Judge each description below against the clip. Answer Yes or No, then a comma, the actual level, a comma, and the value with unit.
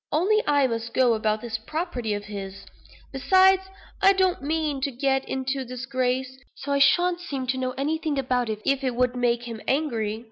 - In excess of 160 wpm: Yes, average, 185 wpm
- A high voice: Yes, very high, 260 Hz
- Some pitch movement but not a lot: Yes, average, 3.7 semitones